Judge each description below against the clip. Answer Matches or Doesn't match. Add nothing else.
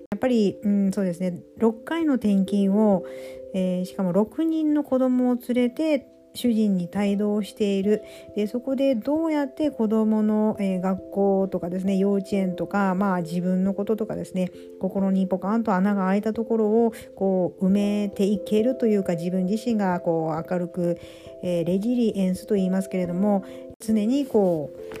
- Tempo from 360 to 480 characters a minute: Doesn't match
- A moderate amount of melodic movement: Matches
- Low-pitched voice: Doesn't match